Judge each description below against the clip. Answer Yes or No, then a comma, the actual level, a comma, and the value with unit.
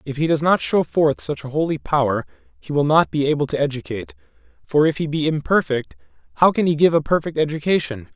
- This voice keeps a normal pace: No, fast, 215 wpm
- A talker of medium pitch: Yes, medium, 150 Hz